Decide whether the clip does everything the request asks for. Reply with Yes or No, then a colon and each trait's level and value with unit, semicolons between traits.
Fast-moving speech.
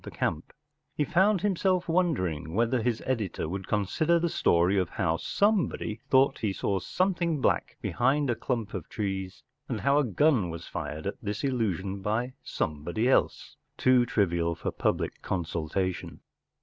No: average, 160 wpm